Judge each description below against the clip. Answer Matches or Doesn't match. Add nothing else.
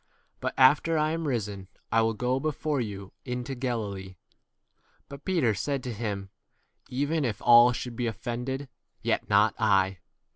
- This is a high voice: Doesn't match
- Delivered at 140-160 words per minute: Doesn't match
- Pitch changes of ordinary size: Matches